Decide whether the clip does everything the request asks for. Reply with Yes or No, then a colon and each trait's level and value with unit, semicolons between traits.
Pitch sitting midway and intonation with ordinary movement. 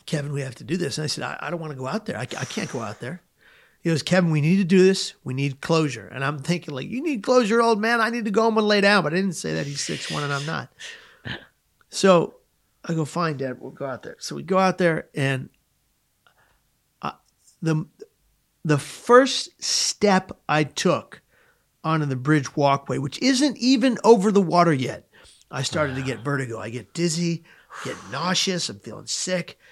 No: medium, 165 Hz; wide, 6.2 semitones